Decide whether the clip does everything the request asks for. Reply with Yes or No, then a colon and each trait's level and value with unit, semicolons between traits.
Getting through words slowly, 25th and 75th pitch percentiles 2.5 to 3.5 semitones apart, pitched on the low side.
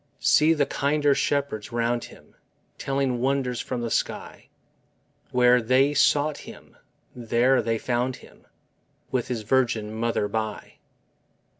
Yes: slow, 125 wpm; average, 2.8 semitones; low, 125 Hz